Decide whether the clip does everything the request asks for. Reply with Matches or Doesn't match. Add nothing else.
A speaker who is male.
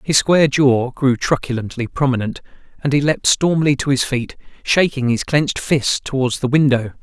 Matches